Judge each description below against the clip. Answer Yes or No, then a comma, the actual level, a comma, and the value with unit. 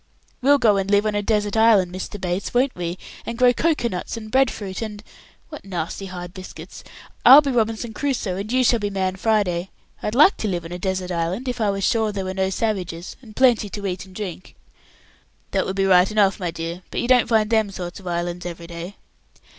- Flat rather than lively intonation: No, average, 3.7 semitones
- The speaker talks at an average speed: No, fast, 225 wpm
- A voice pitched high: Yes, high, 200 Hz